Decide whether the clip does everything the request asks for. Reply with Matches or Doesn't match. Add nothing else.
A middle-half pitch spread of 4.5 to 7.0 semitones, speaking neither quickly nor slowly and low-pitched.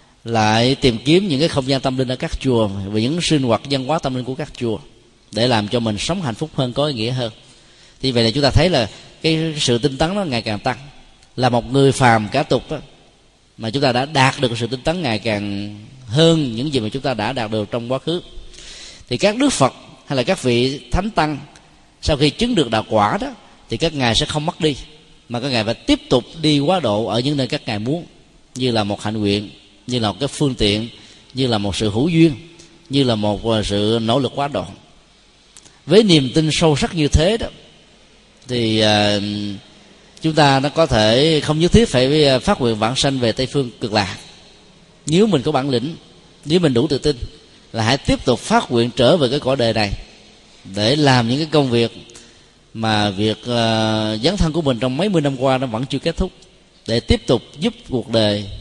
Matches